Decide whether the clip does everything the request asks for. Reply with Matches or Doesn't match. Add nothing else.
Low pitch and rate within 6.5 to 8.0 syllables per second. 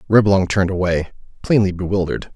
Matches